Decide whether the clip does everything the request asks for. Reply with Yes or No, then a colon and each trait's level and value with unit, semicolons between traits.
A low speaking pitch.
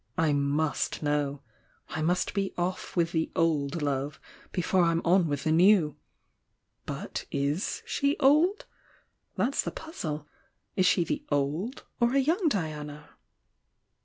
No: medium, 165 Hz